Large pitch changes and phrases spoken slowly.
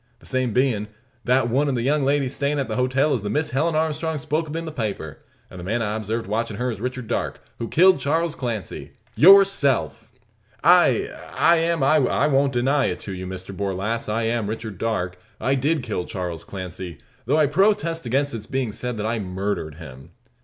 No: wide, 5.9 semitones; fast, 205 wpm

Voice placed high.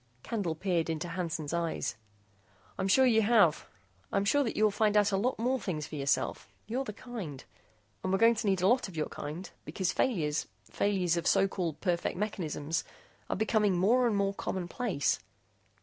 Yes: high, 195 Hz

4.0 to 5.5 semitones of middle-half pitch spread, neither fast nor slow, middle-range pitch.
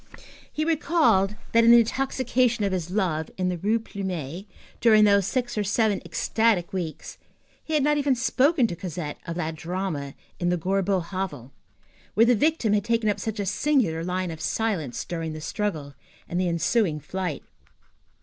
No: average, 5.2 semitones; average, 175 wpm; high, 195 Hz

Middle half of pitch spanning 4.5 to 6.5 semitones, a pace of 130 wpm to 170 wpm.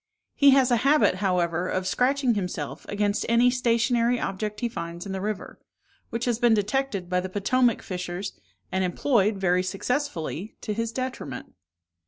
Yes: average, 4.9 semitones; average, 160 wpm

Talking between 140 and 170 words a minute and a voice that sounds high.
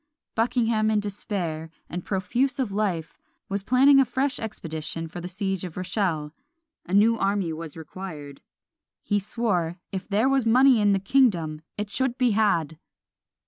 Yes: average, 155 wpm; high, 200 Hz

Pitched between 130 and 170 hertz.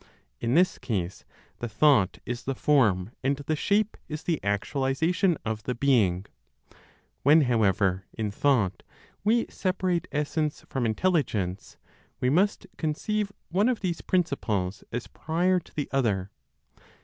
Yes: low, 135 Hz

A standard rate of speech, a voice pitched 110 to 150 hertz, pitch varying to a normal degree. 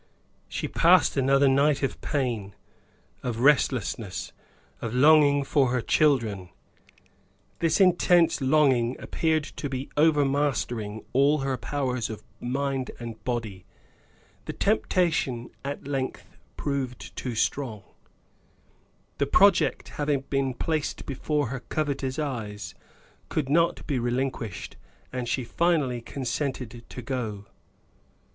No: slow, 110 wpm; low, 135 Hz; average, 3.3 semitones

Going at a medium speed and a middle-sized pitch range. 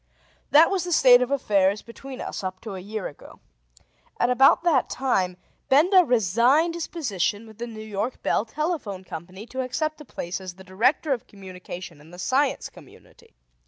No: average, 180 wpm; wide, 6.6 semitones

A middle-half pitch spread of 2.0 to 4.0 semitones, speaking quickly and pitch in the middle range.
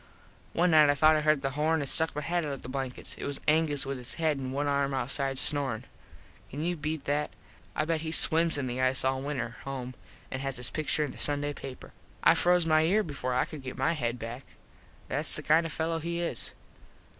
Yes: average, 3.0 semitones; fast, 235 wpm; medium, 145 Hz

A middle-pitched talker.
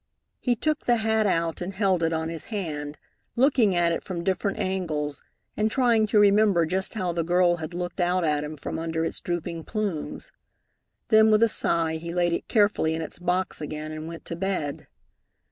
Yes: medium, 175 Hz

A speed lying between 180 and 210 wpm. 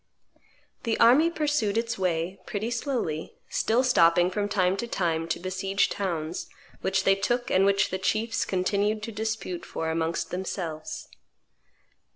No: average, 145 wpm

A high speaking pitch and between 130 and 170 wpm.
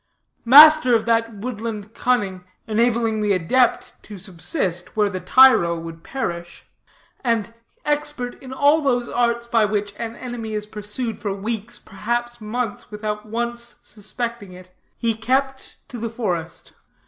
Yes: high, 225 Hz; average, 140 wpm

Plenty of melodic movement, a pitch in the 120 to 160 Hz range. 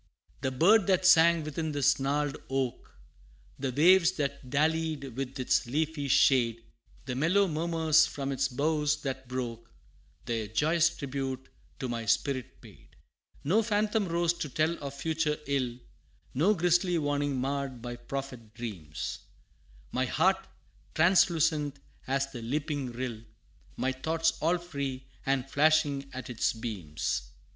No: average, 3.9 semitones; medium, 140 Hz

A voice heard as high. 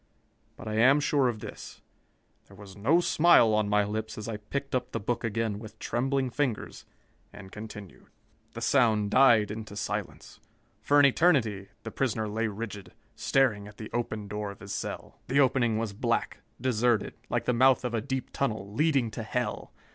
No: low, 115 Hz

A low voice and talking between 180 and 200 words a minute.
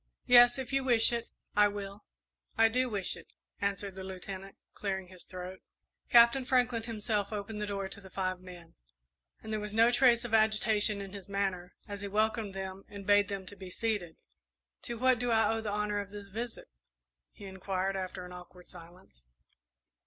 No: high, 205 Hz; average, 185 wpm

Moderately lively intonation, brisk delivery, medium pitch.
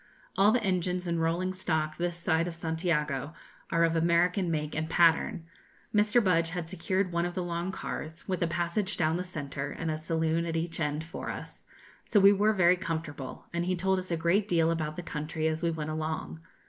No: narrow, 2.2 semitones; fast, 210 wpm; medium, 170 Hz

